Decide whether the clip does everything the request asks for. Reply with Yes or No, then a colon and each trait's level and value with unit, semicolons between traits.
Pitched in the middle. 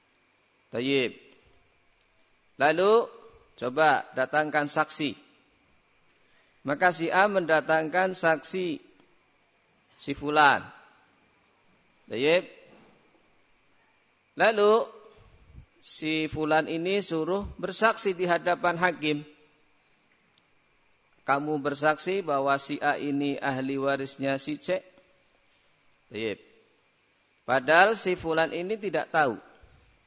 Yes: medium, 160 Hz